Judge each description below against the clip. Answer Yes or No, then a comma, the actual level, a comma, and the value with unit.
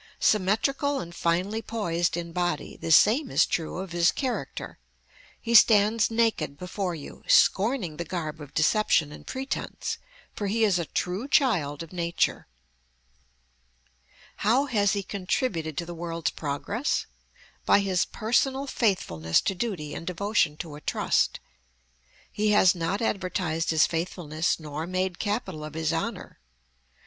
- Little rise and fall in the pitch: No, average, 4.6 semitones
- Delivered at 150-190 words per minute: No, average, 140 wpm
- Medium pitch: Yes, medium, 180 Hz